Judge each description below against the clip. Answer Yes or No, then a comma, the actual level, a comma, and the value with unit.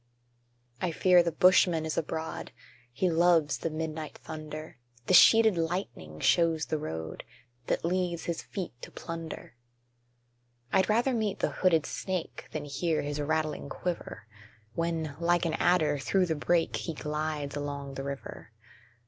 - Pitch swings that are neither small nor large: Yes, average, 3.0 semitones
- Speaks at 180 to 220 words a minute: No, average, 145 wpm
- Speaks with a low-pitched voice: No, medium, 160 Hz